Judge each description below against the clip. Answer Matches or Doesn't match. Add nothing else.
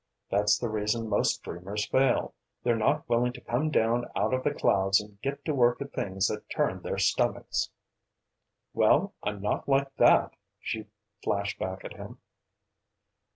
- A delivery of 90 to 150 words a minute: Doesn't match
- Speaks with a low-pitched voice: Matches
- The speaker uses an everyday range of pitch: Matches